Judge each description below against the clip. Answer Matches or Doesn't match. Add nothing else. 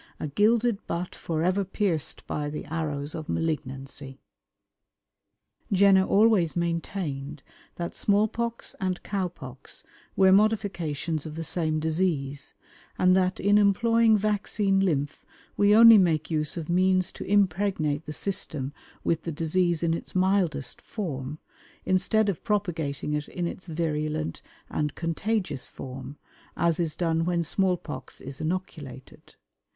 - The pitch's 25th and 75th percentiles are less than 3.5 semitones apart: Doesn't match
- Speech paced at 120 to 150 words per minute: Matches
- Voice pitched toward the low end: Doesn't match